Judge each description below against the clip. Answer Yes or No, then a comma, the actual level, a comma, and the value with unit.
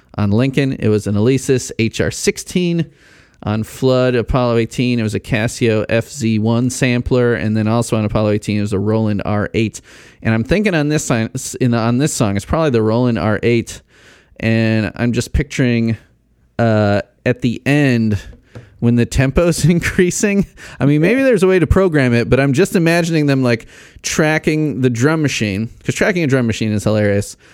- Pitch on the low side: Yes, low, 120 Hz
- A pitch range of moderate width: Yes, average, 4.6 semitones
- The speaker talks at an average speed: Yes, average, 175 wpm